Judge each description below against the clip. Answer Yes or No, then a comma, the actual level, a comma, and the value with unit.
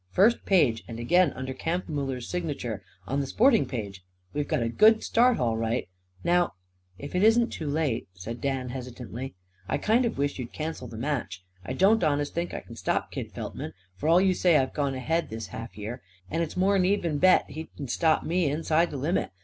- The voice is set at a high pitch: No, medium, 145 Hz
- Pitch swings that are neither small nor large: No, wide, 6.6 semitones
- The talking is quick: Yes, fast, 210 wpm